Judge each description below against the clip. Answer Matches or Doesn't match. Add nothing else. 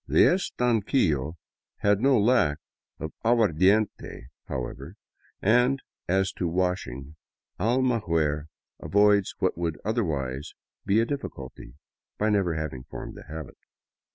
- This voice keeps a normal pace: Doesn't match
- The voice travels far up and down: Matches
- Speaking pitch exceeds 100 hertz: Doesn't match